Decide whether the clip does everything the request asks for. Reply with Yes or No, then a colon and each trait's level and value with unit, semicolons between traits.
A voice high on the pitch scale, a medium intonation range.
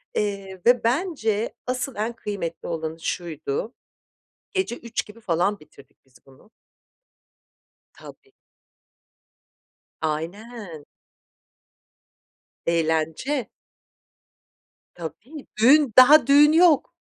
No: high, 215 Hz; wide, 7.6 semitones